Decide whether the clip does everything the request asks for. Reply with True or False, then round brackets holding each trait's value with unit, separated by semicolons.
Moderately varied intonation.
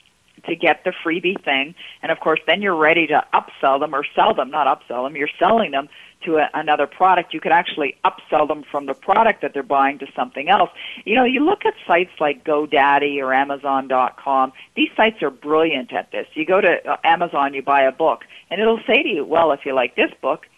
False (5.7 semitones)